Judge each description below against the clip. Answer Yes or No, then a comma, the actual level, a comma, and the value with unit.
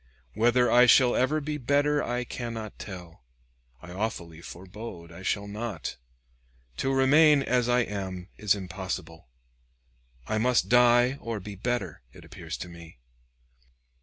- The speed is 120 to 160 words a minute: Yes, slow, 135 wpm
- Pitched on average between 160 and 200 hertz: No, low, 110 Hz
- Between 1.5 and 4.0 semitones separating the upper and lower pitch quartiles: No, average, 5.1 semitones